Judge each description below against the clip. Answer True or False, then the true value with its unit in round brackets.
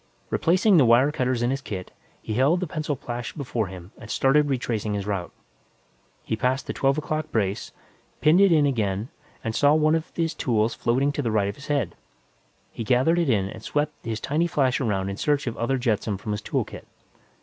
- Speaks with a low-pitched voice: True (125 Hz)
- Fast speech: True (215 wpm)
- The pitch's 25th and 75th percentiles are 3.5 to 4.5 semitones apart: False (5.3 semitones)